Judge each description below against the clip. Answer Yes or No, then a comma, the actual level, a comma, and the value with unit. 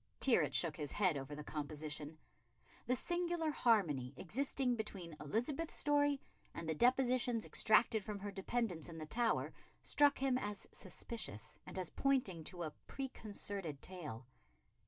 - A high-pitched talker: Yes, high, 205 Hz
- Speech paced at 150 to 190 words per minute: No, average, 140 wpm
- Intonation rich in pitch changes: Yes, wide, 8.2 semitones